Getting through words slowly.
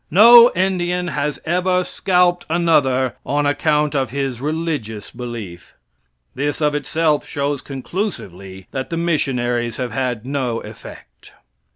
Yes: slow, 120 wpm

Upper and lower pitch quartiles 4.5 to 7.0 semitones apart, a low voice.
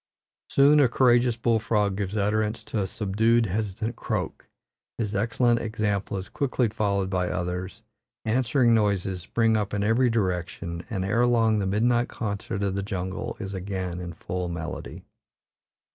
No: average, 3.3 semitones; low, 105 Hz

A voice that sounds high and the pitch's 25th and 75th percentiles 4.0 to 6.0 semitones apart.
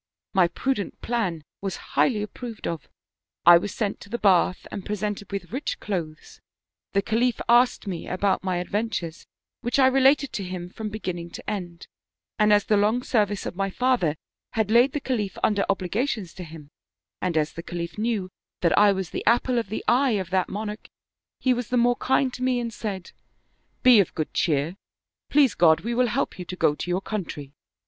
Yes: high, 205 Hz; average, 4.8 semitones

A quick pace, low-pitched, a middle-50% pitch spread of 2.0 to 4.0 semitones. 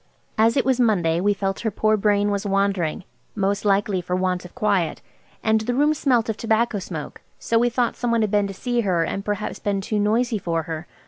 No: fast, 215 wpm; high, 205 Hz; average, 2.9 semitones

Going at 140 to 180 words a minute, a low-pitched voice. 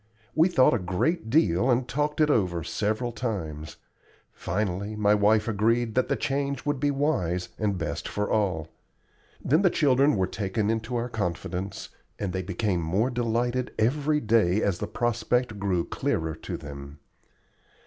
Yes: average, 160 wpm; low, 110 Hz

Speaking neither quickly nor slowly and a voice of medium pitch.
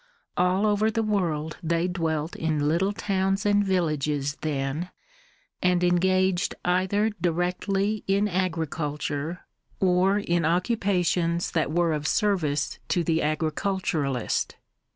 No: slow, 110 wpm; medium, 175 Hz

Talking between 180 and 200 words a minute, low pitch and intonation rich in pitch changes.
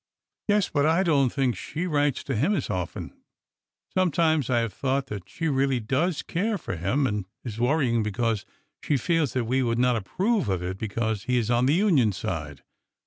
Yes: average, 195 wpm; low, 130 Hz; wide, 6.1 semitones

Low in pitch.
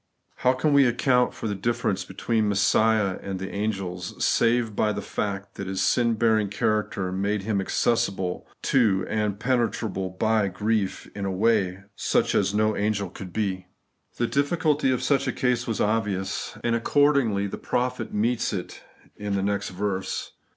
Yes: low, 105 Hz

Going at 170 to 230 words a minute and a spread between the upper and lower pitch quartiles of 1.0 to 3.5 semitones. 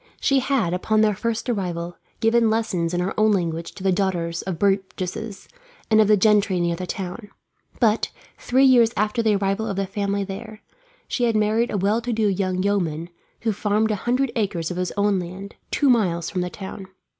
Yes: average, 200 wpm; average, 3.2 semitones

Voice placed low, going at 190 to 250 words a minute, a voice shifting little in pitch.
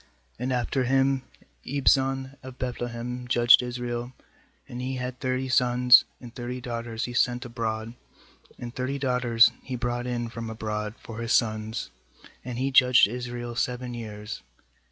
No: low, 125 Hz; average, 150 wpm; narrow, 1.4 semitones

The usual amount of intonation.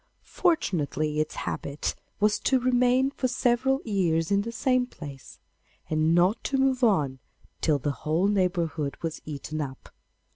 No: wide, 8.2 semitones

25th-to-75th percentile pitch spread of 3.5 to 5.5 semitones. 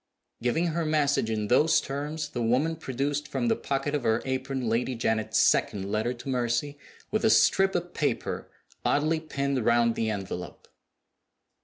Yes: average, 4.6 semitones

